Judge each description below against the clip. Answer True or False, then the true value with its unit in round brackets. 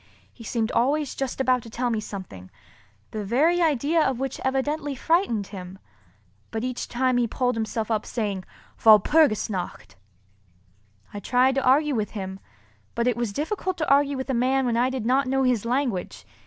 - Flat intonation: False (3.9 semitones)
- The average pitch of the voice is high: True (250 Hz)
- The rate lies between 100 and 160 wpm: False (175 wpm)